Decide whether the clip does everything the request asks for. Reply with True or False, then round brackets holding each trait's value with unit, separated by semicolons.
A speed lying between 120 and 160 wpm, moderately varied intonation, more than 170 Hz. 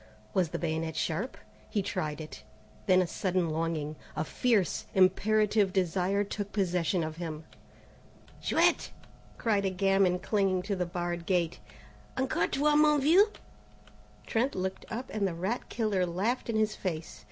True (150 wpm; 3.9 semitones; 190 Hz)